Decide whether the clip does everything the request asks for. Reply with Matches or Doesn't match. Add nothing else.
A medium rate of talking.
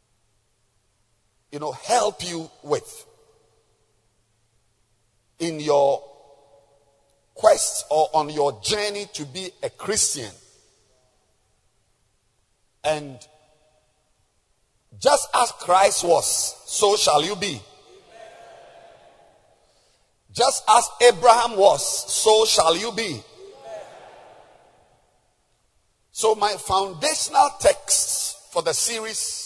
Doesn't match